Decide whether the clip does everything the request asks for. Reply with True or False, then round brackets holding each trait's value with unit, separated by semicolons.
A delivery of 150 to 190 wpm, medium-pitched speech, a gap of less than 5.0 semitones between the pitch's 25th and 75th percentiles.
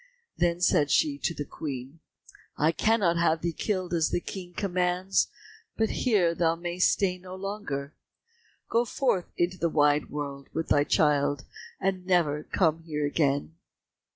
True (155 wpm; 170 Hz; 3.7 semitones)